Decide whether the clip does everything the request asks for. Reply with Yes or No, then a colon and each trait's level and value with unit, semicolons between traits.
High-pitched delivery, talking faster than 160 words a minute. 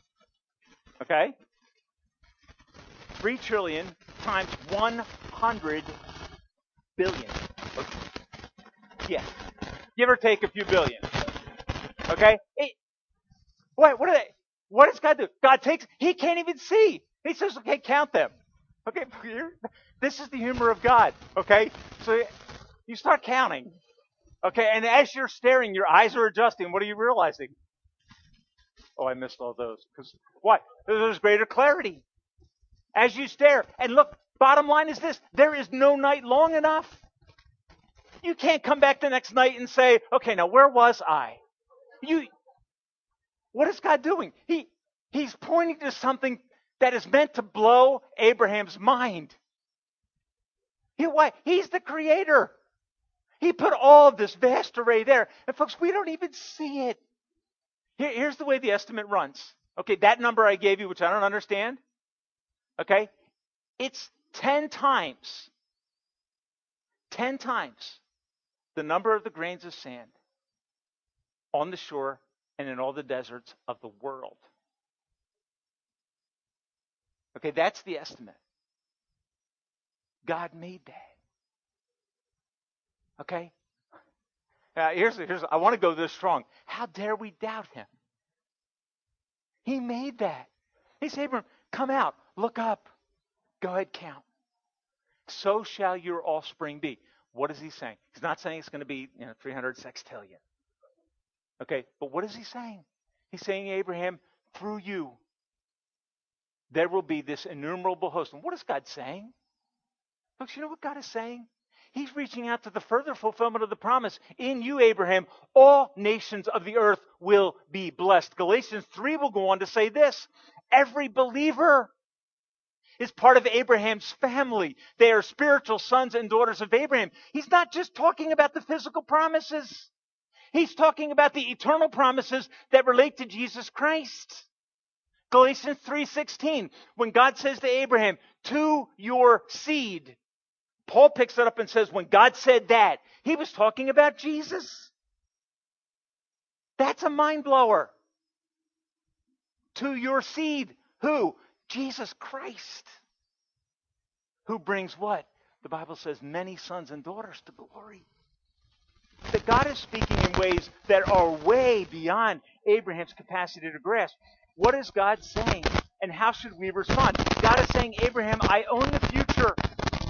No: high, 240 Hz; average, 140 wpm